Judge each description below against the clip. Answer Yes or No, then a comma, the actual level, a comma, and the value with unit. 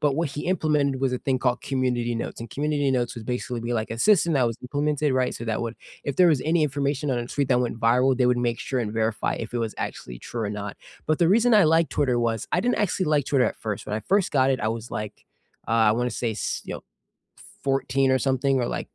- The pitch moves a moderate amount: Yes, average, 3.8 semitones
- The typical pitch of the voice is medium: No, low, 130 Hz